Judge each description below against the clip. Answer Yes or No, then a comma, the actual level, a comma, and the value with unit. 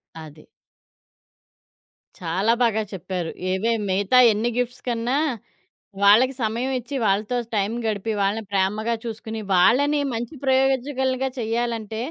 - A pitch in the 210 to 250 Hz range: Yes, high, 225 Hz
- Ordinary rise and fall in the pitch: Yes, average, 3.7 semitones